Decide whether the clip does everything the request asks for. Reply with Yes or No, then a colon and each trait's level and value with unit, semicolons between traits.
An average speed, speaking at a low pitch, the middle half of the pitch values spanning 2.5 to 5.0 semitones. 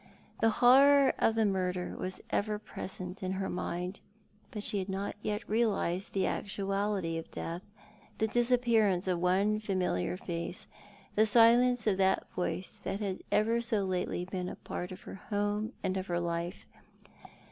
No: average, 155 wpm; high, 195 Hz; average, 3.1 semitones